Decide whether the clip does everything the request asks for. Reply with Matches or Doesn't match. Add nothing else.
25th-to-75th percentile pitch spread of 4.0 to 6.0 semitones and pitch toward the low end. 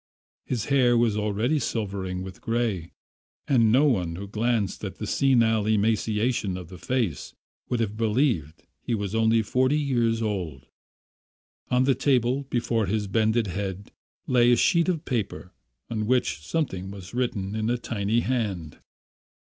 Doesn't match